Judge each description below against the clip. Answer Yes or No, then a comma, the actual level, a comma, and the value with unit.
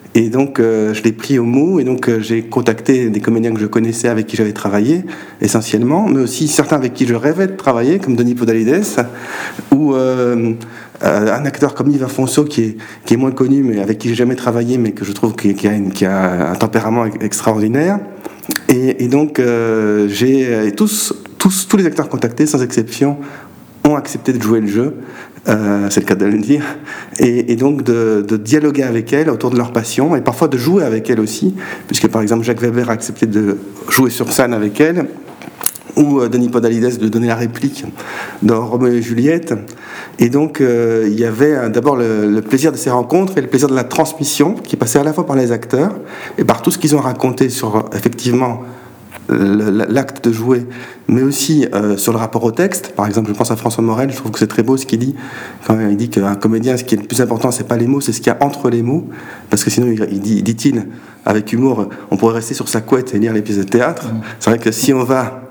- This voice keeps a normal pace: No, fast, 230 wpm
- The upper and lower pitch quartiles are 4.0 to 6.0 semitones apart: No, average, 3.2 semitones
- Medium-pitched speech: No, low, 120 Hz